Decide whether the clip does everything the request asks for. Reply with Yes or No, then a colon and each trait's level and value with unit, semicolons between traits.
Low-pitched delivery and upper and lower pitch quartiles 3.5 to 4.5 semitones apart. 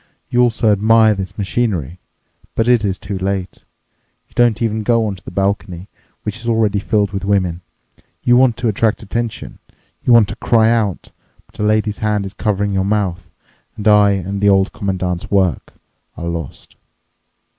No: low, 105 Hz; narrow, 2.5 semitones